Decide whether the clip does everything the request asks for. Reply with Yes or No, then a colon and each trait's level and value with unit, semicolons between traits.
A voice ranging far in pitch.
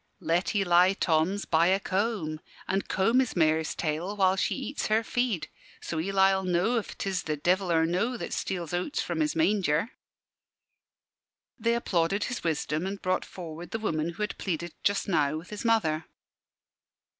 No: average, 4.1 semitones